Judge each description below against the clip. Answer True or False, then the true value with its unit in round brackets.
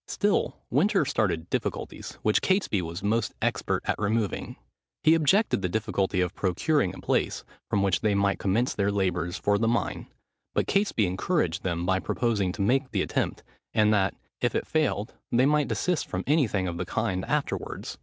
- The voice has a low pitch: True (100 Hz)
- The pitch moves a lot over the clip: False (4.6 semitones)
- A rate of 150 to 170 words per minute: False (180 wpm)